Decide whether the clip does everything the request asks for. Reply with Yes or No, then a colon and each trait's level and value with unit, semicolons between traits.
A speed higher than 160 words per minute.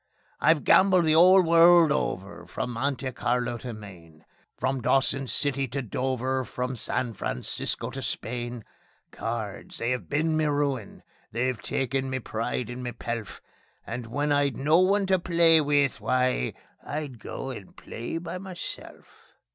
No: average, 155 wpm